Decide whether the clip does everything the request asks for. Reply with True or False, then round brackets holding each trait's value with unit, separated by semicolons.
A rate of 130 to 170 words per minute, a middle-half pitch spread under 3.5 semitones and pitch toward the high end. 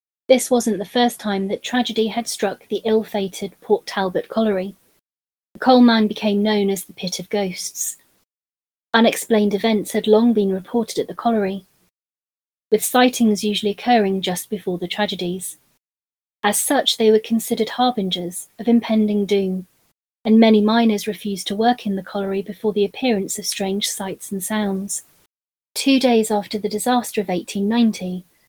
True (160 wpm; 2.5 semitones; 210 Hz)